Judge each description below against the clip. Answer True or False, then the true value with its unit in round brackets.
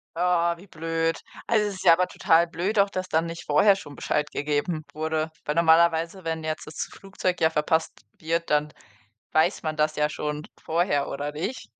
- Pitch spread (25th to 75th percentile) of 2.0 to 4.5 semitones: True (2.5 semitones)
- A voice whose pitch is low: False (165 Hz)